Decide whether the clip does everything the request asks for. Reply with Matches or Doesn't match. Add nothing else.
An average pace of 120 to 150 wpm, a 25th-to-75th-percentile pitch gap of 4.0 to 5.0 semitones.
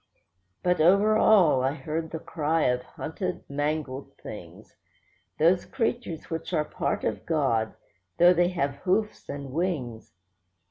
Matches